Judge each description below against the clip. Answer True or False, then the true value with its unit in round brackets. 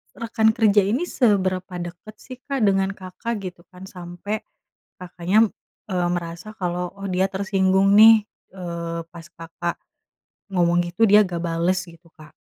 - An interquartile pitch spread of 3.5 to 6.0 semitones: False (3.1 semitones)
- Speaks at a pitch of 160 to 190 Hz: True (185 Hz)